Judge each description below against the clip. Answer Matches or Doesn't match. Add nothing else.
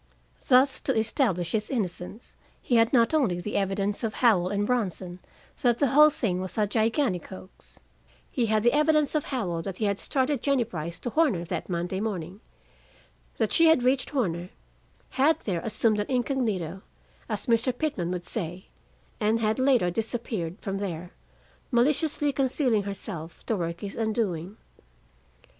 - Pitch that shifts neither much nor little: Doesn't match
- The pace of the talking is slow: Doesn't match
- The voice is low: Doesn't match